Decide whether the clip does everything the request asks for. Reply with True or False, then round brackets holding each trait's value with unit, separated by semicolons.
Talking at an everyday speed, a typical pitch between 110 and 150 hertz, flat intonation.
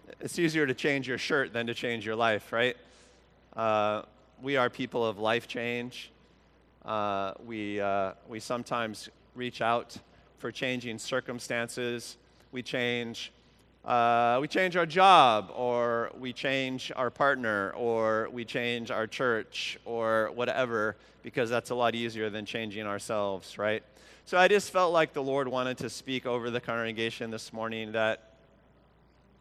True (150 wpm; 120 Hz; 2.3 semitones)